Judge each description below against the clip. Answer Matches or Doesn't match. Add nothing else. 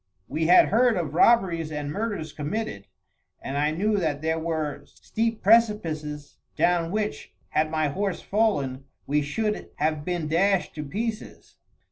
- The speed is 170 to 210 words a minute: Doesn't match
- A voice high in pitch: Doesn't match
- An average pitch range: Doesn't match